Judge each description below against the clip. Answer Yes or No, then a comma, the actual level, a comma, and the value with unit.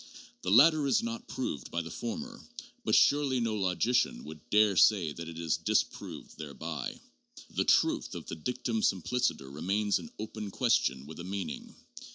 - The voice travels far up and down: Yes, wide, 7.3 semitones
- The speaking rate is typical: Yes, average, 165 wpm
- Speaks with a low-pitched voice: Yes, low, 105 Hz